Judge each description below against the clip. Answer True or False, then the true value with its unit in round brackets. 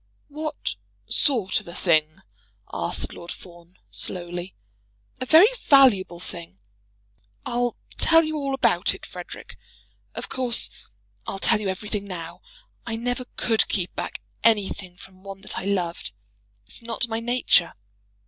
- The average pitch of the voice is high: True (200 Hz)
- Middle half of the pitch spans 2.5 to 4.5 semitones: False (5.6 semitones)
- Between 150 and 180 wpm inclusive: False (140 wpm)